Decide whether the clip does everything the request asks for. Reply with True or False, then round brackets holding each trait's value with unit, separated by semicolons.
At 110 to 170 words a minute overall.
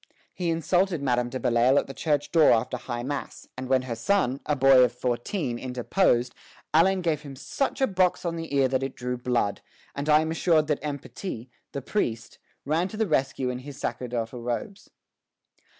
False (195 wpm)